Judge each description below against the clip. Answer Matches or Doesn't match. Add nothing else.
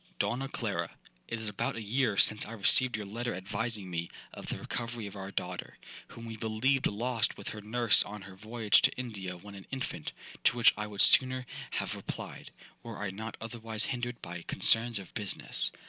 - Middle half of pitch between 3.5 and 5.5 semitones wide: Doesn't match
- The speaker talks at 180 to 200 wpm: Matches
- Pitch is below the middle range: Matches